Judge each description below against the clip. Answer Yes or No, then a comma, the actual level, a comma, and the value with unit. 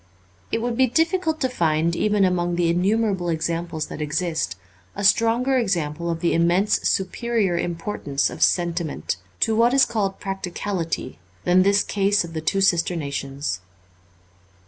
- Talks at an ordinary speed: Yes, average, 150 wpm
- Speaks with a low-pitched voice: No, medium, 180 Hz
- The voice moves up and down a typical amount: Yes, average, 4.1 semitones